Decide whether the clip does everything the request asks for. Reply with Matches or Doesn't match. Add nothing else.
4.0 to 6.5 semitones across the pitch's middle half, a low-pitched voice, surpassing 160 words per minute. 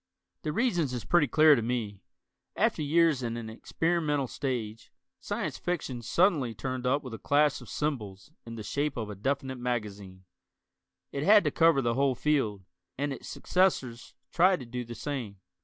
Matches